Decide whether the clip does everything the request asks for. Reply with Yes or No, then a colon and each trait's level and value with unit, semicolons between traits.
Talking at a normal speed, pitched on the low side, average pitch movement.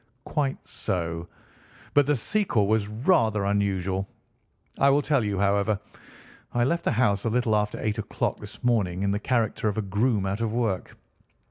Yes: average, 170 wpm; low, 105 Hz; average, 3.5 semitones